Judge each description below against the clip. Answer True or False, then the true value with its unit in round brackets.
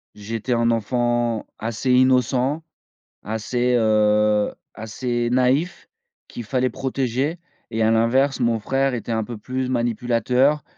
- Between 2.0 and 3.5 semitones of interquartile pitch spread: True (2.5 semitones)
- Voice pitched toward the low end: True (120 Hz)